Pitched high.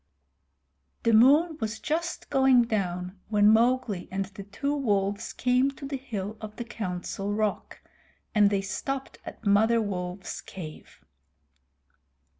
Yes: high, 215 Hz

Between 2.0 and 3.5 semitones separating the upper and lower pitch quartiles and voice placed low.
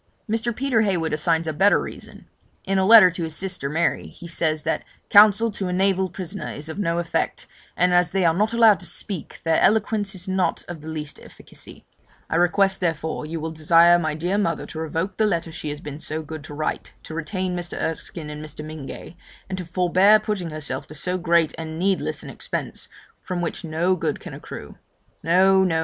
No: average, 3.2 semitones; medium, 175 Hz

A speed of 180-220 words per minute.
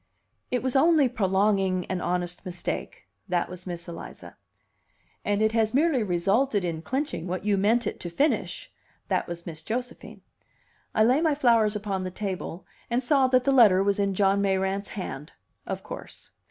No: average, 170 wpm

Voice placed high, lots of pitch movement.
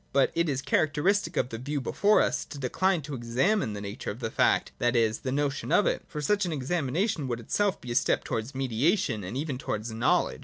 No: low, 135 Hz; wide, 6.0 semitones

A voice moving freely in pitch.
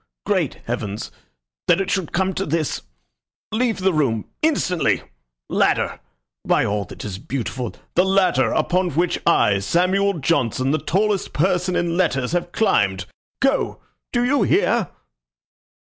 Yes: wide, 6.8 semitones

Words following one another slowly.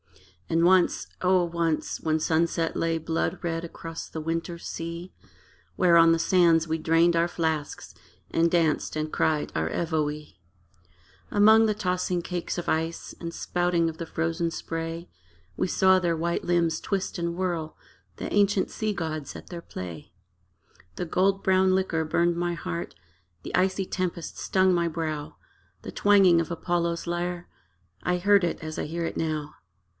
No: average, 160 wpm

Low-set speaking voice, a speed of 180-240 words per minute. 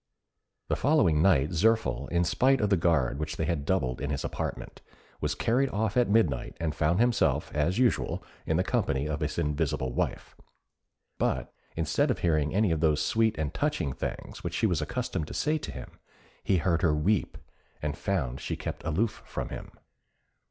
Yes: very low, 85 Hz; average, 185 wpm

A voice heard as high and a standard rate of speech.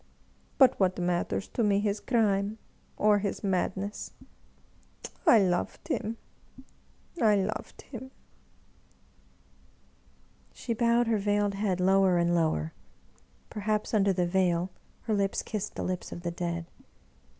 No: high, 200 Hz; slow, 130 wpm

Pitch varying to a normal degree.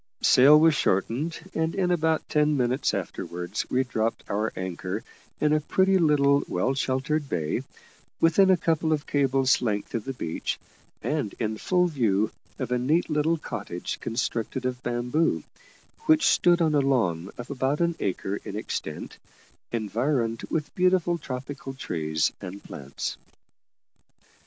No: wide, 6.0 semitones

